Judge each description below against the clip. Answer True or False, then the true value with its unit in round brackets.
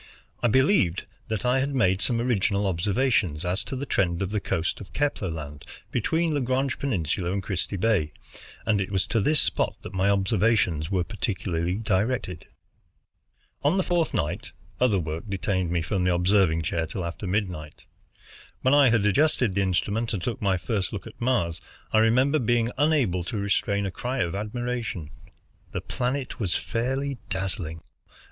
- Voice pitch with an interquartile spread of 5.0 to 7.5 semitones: True (5.4 semitones)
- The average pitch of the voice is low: True (100 Hz)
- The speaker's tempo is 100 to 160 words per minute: False (170 wpm)